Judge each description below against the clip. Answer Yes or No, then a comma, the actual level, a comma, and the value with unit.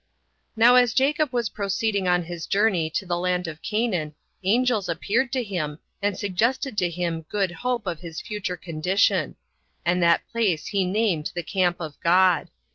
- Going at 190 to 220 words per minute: No, average, 175 wpm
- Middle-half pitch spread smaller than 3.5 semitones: No, average, 4.2 semitones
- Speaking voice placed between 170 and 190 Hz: Yes, medium, 185 Hz